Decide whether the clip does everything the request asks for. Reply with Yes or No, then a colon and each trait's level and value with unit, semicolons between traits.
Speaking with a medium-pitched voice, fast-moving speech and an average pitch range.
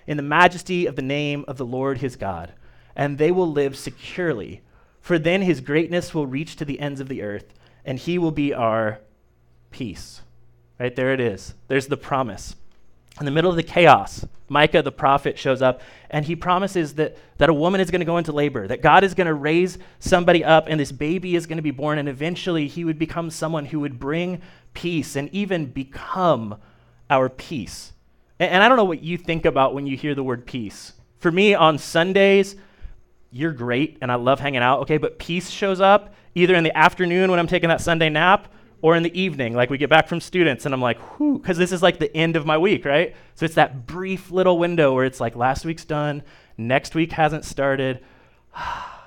Yes: medium, 150 Hz; fast, 215 wpm; average, 4.7 semitones